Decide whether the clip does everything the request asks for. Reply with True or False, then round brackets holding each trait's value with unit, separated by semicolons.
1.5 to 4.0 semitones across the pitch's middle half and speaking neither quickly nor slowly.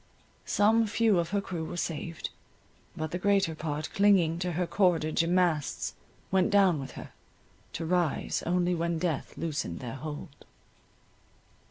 True (2.9 semitones; 150 wpm)